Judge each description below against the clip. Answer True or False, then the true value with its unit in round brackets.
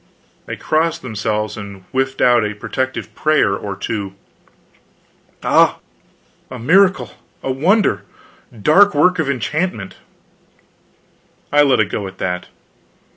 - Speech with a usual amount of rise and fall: False (7.0 semitones)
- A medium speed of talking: False (125 wpm)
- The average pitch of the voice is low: True (130 Hz)